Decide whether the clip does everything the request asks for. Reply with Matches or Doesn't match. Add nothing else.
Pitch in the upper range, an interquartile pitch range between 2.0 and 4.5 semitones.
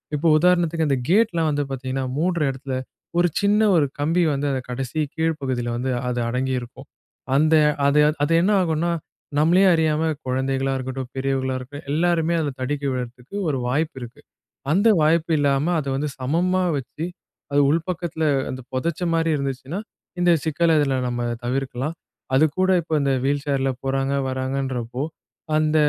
Doesn't match